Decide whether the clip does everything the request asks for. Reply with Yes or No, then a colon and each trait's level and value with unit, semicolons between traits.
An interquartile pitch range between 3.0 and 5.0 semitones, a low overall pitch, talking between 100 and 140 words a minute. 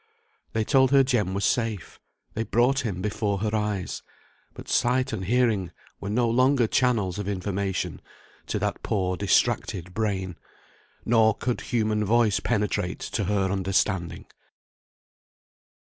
Yes: average, 3.6 semitones; low, 105 Hz; slow, 135 wpm